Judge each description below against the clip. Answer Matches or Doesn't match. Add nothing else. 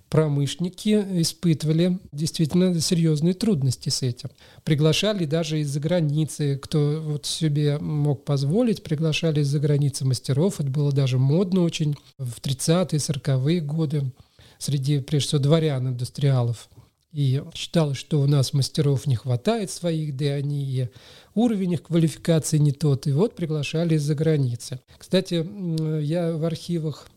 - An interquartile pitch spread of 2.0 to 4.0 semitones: Matches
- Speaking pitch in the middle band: Matches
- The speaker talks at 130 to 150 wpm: Matches